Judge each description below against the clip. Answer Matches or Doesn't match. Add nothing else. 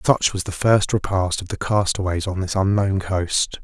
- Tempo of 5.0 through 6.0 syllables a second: Doesn't match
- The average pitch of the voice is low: Matches